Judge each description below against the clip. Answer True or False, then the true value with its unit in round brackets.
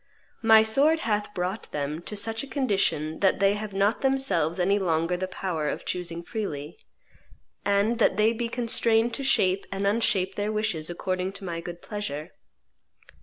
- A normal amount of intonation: True (4.0 semitones)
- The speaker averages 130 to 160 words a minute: False (170 wpm)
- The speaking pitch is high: True (200 Hz)